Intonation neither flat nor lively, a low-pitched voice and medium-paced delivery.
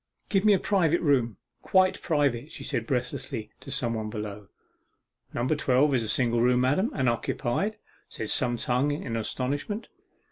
Yes: average, 4.4 semitones; low, 130 Hz; average, 165 wpm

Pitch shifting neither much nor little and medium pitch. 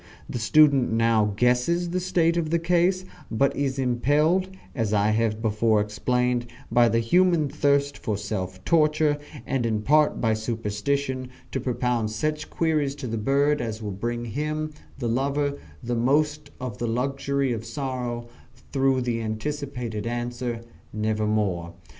No: average, 4.5 semitones; low, 125 Hz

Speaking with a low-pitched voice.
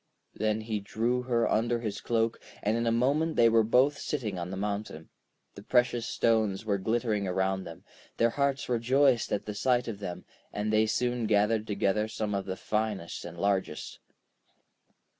Yes: low, 110 Hz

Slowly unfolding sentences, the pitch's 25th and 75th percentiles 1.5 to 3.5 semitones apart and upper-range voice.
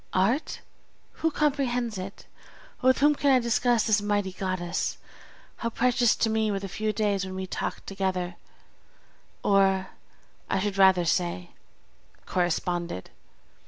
No: slow, 130 wpm; average, 4.0 semitones; high, 200 Hz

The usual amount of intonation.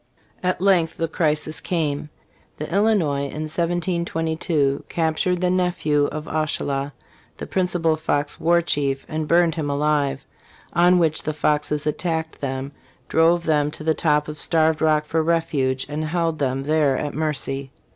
No: narrow, 2.3 semitones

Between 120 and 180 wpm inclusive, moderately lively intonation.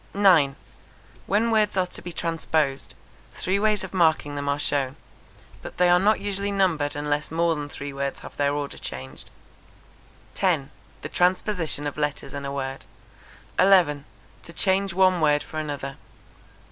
Yes: average, 160 wpm; average, 4.7 semitones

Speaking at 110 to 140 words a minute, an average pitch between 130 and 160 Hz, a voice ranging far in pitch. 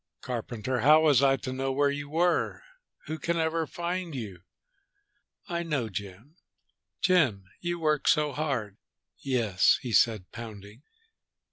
Yes: slow, 135 wpm; low, 135 Hz; wide, 6.1 semitones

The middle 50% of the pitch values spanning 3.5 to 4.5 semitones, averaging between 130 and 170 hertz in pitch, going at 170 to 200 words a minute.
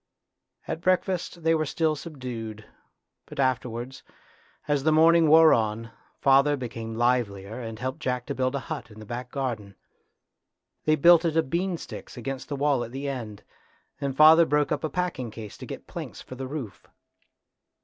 No: average, 4.9 semitones; low, 135 Hz; average, 175 wpm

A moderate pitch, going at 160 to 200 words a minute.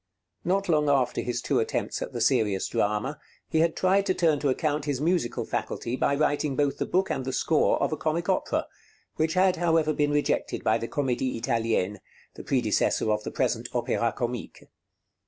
Yes: medium, 145 Hz; average, 190 wpm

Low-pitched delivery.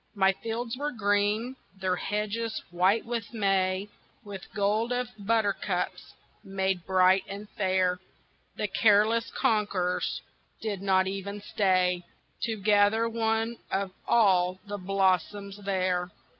No: high, 200 Hz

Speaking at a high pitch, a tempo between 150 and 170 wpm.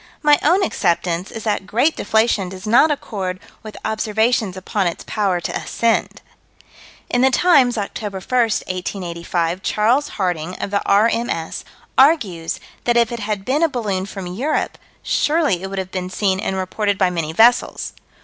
Yes: high, 205 Hz; average, 160 wpm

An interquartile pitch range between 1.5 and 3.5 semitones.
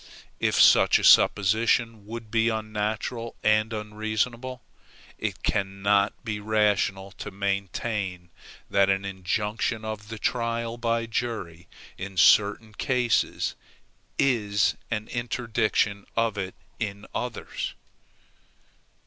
Yes: narrow, 2.4 semitones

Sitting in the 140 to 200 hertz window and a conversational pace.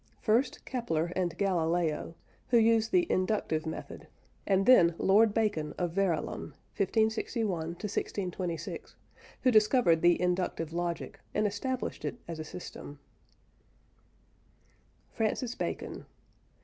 No: high, 190 Hz; slow, 110 wpm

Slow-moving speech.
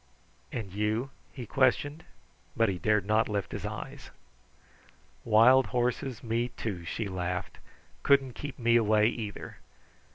Yes: slow, 130 wpm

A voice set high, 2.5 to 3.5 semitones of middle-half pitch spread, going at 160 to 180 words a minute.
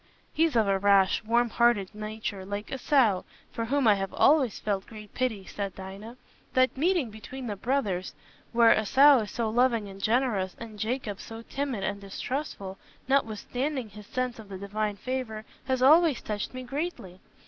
No: high, 225 Hz; average, 4.2 semitones; average, 170 wpm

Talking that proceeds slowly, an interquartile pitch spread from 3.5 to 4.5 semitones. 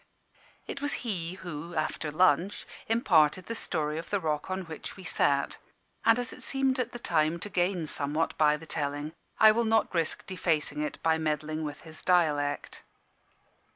No: average, 175 wpm; average, 4.1 semitones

